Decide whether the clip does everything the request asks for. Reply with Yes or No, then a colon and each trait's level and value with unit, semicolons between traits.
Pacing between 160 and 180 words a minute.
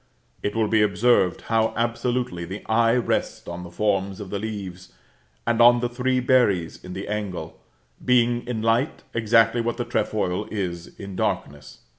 Yes: average, 165 wpm